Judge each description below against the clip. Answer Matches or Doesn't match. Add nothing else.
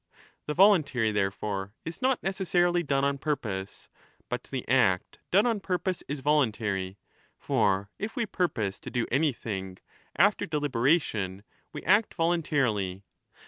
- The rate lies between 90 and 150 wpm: Matches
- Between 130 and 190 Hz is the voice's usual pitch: Matches